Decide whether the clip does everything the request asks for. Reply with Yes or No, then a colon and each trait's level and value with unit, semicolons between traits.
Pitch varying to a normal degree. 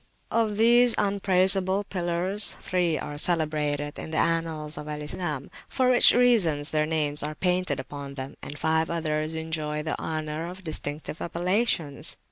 Yes: average, 3.6 semitones